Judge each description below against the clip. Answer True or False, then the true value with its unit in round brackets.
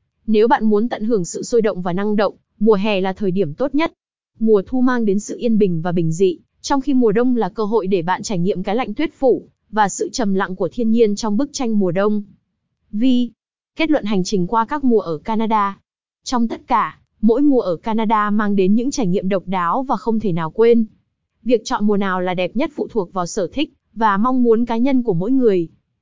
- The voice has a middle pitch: False (220 Hz)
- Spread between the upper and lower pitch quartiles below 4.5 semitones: True (3.6 semitones)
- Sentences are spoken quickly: False (240 wpm)